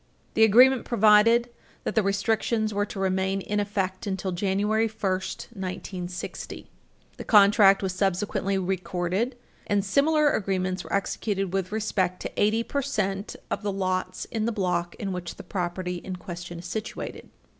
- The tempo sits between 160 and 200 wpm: No, average, 150 wpm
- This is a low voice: No, high, 195 Hz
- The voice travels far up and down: No, narrow, 2.6 semitones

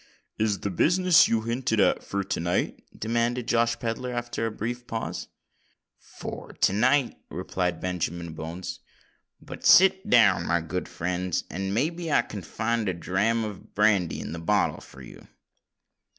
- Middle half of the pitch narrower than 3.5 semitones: No, average, 4.9 semitones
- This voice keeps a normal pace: Yes, average, 160 wpm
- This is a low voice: Yes, low, 105 Hz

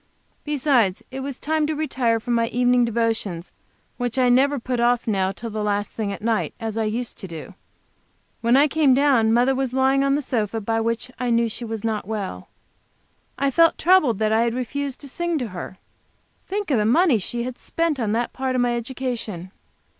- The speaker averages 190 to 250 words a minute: Yes, fast, 205 wpm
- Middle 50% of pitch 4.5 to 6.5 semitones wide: No, average, 3.3 semitones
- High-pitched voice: Yes, high, 240 Hz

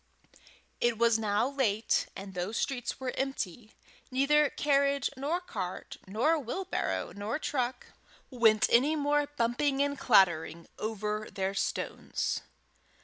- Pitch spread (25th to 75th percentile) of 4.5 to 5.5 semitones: Yes, average, 4.9 semitones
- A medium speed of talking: No, slow, 115 wpm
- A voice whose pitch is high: Yes, high, 240 Hz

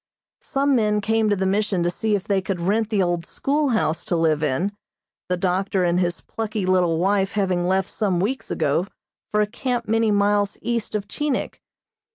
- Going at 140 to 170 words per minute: No, average, 190 wpm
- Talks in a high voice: Yes, high, 200 Hz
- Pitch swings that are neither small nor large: Yes, average, 3.3 semitones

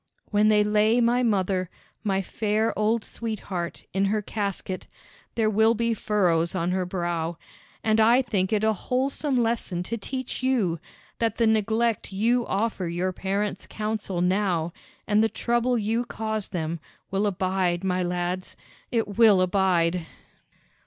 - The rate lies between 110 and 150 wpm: Yes, average, 145 wpm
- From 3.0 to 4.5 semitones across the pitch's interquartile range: Yes, average, 3.4 semitones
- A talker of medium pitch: No, high, 205 Hz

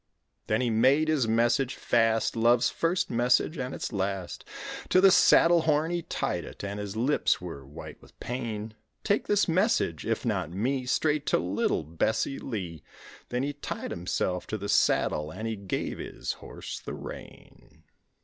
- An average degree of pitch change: No, wide, 6.3 semitones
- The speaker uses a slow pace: No, average, 170 wpm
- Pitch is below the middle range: Yes, low, 115 Hz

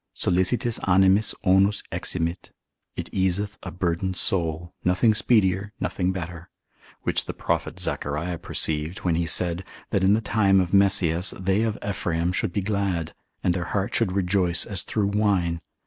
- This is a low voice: Yes, very low, 95 Hz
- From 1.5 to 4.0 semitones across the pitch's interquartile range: Yes, narrow, 2.5 semitones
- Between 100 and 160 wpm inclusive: Yes, average, 155 wpm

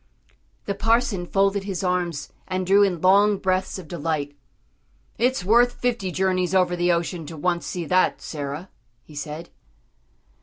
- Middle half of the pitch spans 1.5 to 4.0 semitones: Yes, narrow, 2.6 semitones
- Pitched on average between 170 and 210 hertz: Yes, medium, 185 Hz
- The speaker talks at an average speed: Yes, average, 150 wpm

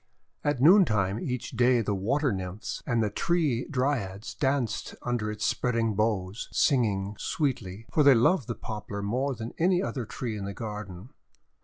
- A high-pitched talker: No, low, 115 Hz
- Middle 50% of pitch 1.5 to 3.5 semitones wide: No, average, 4.5 semitones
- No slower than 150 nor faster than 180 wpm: Yes, average, 160 wpm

